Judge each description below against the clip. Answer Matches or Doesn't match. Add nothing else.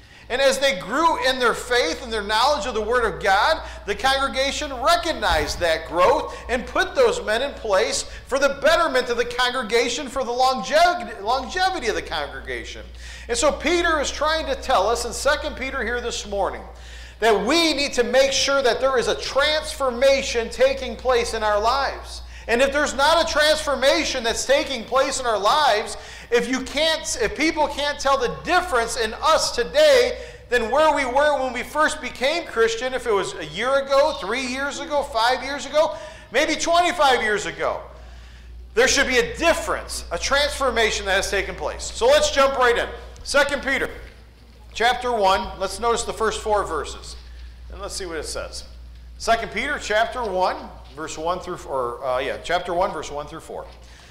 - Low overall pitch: Doesn't match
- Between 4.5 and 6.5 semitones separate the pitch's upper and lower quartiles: Matches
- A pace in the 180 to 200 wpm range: Matches